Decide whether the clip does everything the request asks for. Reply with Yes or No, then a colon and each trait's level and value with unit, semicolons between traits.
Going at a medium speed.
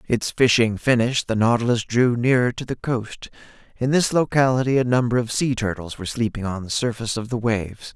Yes: average, 195 wpm